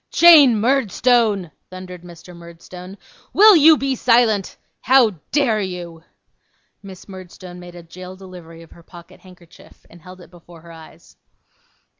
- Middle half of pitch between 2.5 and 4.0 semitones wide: No, average, 4.8 semitones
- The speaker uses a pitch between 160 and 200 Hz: Yes, medium, 185 Hz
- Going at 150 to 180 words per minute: No, average, 140 wpm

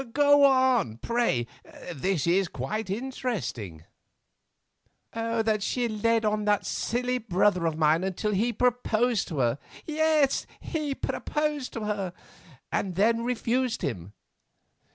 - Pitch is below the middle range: No, high, 215 Hz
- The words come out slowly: Yes, slow, 110 wpm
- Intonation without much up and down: No, wide, 5.6 semitones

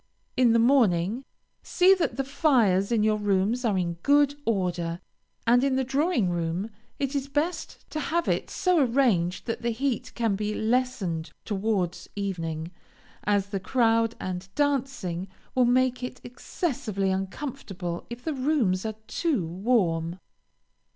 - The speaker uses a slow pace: No, average, 145 wpm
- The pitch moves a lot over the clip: Yes, wide, 6.0 semitones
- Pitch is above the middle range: Yes, high, 225 Hz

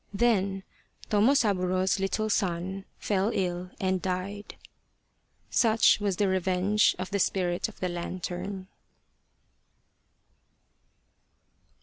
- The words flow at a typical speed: No, slow, 90 wpm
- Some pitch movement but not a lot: No, narrow, 1.9 semitones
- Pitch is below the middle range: No, high, 190 Hz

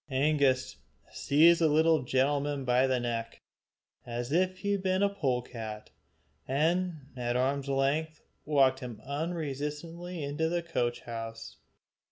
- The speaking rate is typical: No, slow, 130 wpm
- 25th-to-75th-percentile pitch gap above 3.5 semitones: Yes, average, 4.3 semitones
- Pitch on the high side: No, medium, 140 Hz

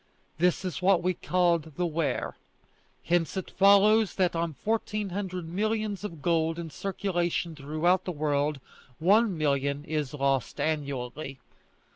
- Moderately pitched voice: Yes, medium, 170 Hz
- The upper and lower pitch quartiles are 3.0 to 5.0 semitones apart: Yes, average, 3.9 semitones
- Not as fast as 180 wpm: Yes, slow, 135 wpm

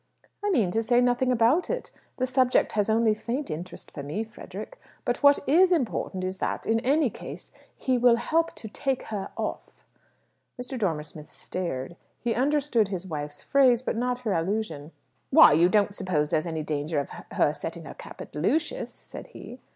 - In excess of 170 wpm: Yes, average, 190 wpm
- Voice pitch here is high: Yes, high, 225 Hz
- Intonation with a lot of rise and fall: Yes, wide, 6.6 semitones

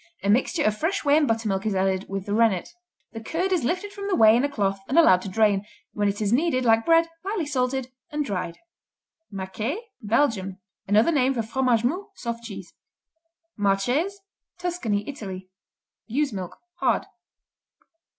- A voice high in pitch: Yes, high, 230 Hz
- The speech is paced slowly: No, average, 170 wpm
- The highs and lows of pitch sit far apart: Yes, wide, 6.7 semitones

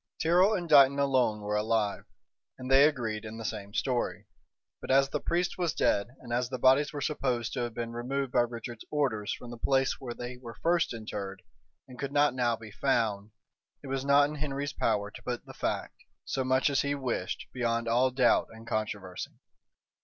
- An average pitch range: Yes, average, 3.4 semitones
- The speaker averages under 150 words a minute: No, average, 200 wpm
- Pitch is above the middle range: No, low, 125 Hz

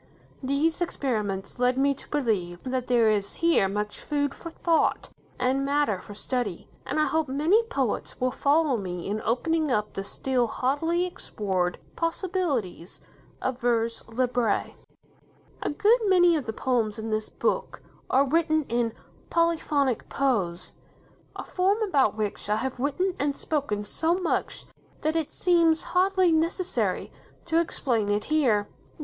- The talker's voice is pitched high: Yes, very high, 265 Hz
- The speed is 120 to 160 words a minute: Yes, average, 145 wpm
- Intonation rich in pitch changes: Yes, wide, 6.9 semitones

